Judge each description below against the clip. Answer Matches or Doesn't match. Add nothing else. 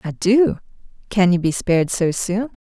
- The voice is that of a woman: Matches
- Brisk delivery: Doesn't match